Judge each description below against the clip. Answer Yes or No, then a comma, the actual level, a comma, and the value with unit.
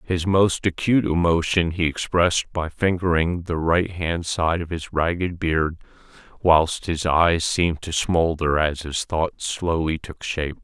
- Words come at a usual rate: Yes, average, 150 wpm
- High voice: No, very low, 85 Hz